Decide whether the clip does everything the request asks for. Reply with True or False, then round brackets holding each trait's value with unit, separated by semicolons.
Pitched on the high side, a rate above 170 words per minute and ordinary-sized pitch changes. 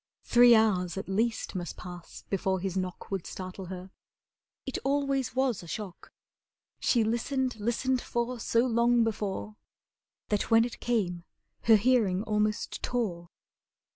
False (220 Hz; 140 wpm; 4.2 semitones)